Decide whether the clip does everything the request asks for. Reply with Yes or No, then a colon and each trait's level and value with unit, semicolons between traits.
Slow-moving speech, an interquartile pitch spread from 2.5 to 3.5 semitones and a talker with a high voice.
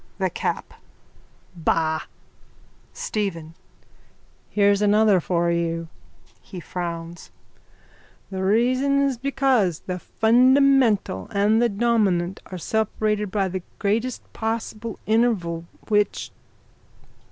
No: slow, 95 wpm; average, 4.8 semitones; high, 205 Hz